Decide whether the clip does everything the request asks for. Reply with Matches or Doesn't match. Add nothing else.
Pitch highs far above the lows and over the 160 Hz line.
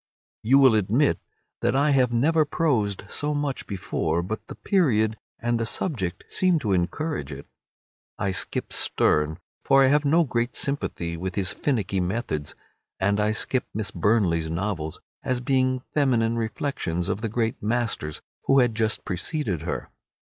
Doesn't match